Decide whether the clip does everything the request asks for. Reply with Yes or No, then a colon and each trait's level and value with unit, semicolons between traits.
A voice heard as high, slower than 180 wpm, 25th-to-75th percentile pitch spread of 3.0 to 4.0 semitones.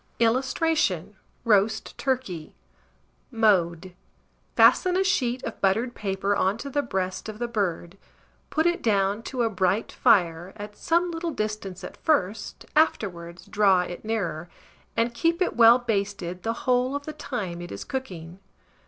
No: high, 215 Hz; average, 150 wpm; wide, 5.4 semitones